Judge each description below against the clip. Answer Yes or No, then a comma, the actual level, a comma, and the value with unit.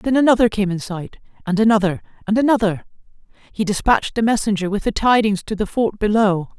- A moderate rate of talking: Yes, average, 180 wpm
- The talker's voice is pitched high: Yes, high, 210 Hz